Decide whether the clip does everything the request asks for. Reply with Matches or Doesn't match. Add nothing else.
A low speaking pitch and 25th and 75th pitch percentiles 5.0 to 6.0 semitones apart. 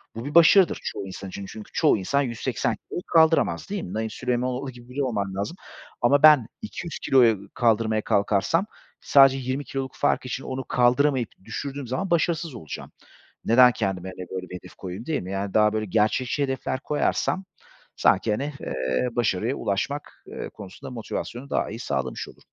Matches